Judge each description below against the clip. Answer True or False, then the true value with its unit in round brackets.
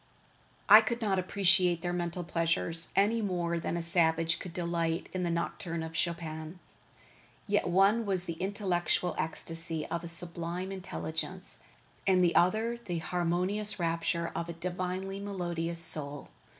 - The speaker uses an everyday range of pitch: False (2.2 semitones)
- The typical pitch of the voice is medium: True (175 Hz)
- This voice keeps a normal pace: True (145 wpm)